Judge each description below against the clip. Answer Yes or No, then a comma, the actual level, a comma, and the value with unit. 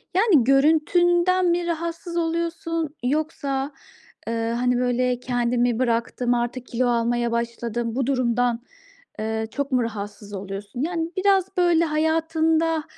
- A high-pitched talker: Yes, very high, 265 Hz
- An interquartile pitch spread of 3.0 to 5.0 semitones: No, wide, 5.6 semitones